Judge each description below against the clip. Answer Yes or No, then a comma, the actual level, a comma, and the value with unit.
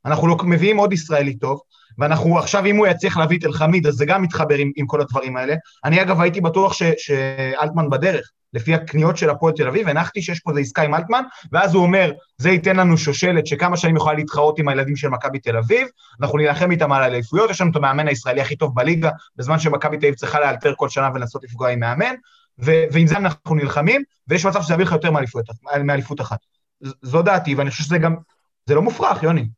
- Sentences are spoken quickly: Yes, fast, 195 wpm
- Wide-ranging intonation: No, average, 3.6 semitones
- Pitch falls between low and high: Yes, medium, 155 Hz